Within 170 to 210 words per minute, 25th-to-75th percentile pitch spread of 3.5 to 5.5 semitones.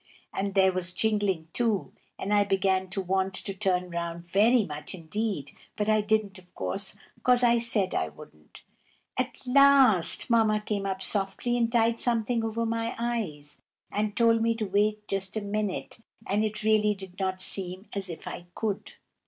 No: average, 175 wpm; average, 3.0 semitones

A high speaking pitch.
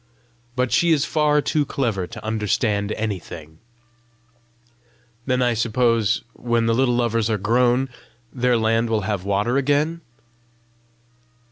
No: low, 115 Hz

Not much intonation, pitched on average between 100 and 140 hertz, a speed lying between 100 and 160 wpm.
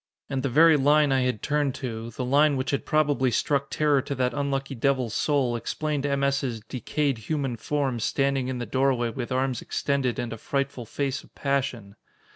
No: narrow, 2.1 semitones; low, 135 Hz; average, 190 wpm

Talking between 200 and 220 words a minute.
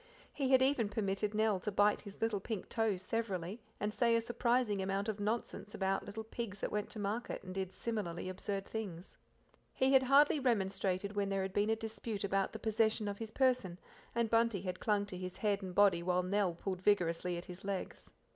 Yes: fast, 205 wpm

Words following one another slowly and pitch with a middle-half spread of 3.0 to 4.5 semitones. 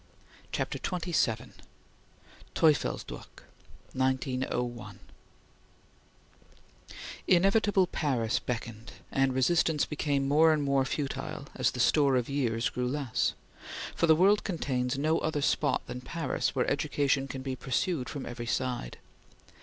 Yes: slow, 115 wpm; average, 3.8 semitones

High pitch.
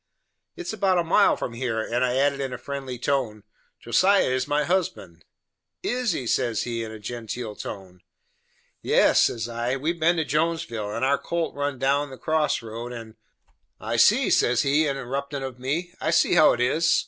No: low, 135 Hz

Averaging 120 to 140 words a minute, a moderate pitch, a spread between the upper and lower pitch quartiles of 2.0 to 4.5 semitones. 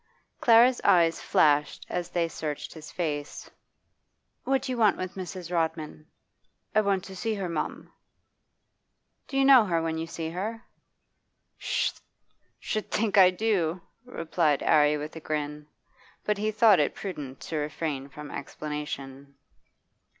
No: slow, 135 wpm; medium, 165 Hz; average, 5.2 semitones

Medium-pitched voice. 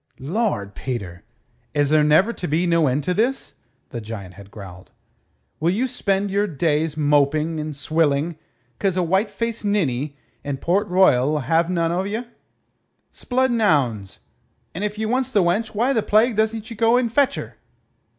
Yes: medium, 170 Hz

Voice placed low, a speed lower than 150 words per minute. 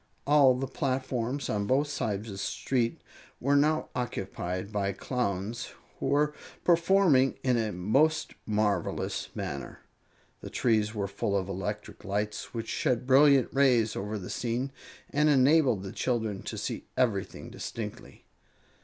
Yes: low, 120 Hz; average, 140 wpm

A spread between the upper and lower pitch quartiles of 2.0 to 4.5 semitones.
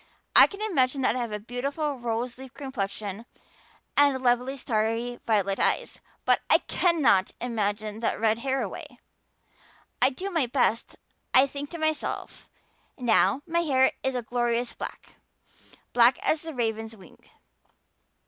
Yes: average, 3.7 semitones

